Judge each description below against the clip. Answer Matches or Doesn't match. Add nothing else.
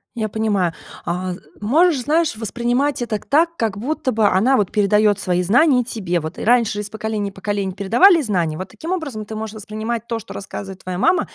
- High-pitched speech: Matches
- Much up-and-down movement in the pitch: Doesn't match